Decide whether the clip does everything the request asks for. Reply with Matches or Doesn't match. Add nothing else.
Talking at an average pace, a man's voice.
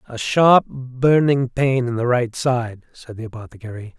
Matches